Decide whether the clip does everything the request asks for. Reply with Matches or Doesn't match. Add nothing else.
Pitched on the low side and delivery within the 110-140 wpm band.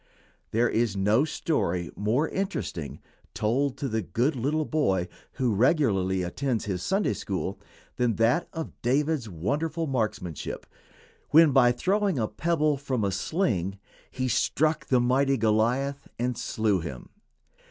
Matches